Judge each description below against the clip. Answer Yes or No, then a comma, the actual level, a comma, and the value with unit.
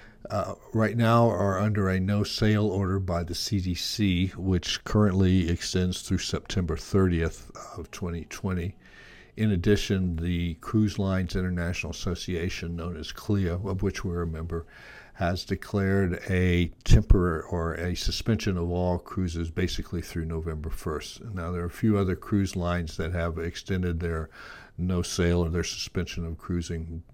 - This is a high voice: No, very low, 90 Hz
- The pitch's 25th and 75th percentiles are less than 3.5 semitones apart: Yes, narrow, 2.4 semitones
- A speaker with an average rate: Yes, average, 145 wpm